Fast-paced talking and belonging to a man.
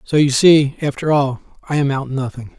Yes: fast, 210 wpm; male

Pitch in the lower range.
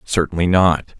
Yes: very low, 85 Hz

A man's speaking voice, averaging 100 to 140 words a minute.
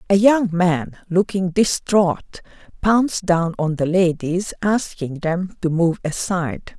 No: female; slow, 135 wpm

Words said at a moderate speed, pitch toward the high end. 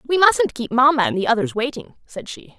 No: fast, 230 wpm; very high, 250 Hz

